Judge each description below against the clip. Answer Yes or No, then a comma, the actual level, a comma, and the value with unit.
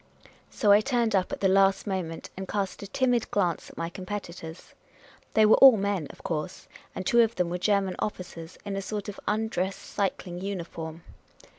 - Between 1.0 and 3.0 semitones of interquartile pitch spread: Yes, narrow, 2.6 semitones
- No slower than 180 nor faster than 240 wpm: Yes, average, 190 wpm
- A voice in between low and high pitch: No, high, 195 Hz